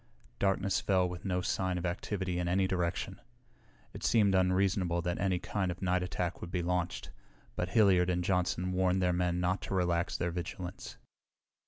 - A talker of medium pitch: No, very low, 90 Hz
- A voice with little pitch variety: Yes, narrow, 1.1 semitones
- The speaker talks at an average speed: Yes, average, 175 wpm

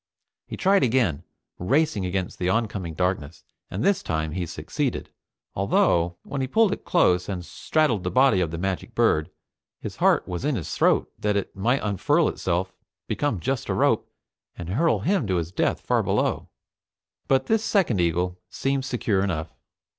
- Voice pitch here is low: Yes, very low, 95 Hz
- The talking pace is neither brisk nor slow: Yes, average, 170 wpm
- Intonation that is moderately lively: No, wide, 6.9 semitones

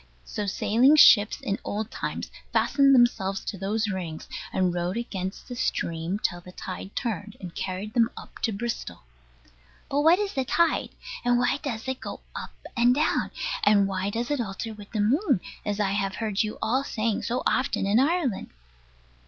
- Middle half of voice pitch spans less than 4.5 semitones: Yes, average, 4.1 semitones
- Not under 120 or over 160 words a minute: No, average, 175 wpm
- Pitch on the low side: No, high, 215 Hz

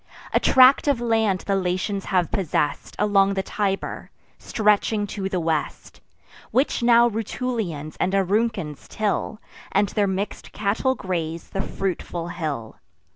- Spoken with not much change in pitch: No, average, 3.5 semitones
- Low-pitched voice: No, high, 195 Hz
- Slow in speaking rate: Yes, slow, 130 wpm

